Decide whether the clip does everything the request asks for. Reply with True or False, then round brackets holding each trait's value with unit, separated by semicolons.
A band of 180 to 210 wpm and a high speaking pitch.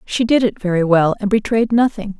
False (220 wpm; 210 Hz)